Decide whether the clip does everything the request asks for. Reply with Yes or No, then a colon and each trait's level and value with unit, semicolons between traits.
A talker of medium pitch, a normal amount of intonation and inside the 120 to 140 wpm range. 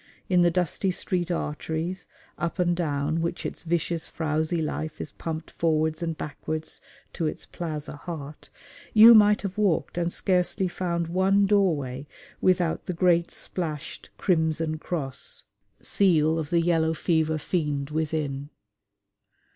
No: medium, 165 Hz; narrow, 2.3 semitones; slow, 135 wpm